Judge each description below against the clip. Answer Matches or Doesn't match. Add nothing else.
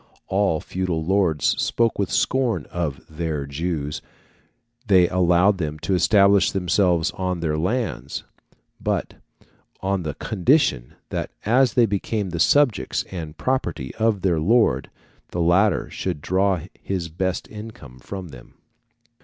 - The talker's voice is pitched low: Matches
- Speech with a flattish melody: Doesn't match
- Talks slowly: Matches